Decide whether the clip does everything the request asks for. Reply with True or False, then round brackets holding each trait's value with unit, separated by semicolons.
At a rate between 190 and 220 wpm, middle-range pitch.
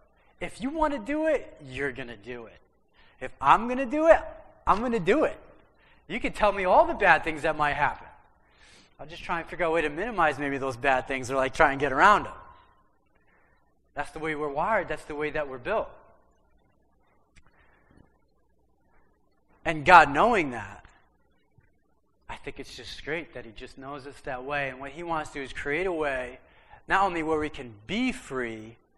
True (205 wpm; 150 Hz)